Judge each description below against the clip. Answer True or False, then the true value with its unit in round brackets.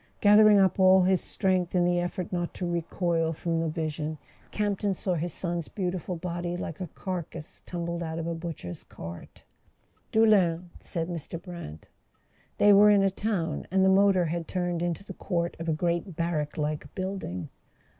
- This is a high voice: False (175 Hz)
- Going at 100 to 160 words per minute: False (175 wpm)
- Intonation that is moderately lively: False (2.3 semitones)